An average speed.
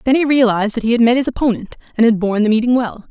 No: fast, 290 wpm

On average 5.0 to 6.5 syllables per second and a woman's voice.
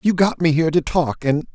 No: 5.7 syllables/s; male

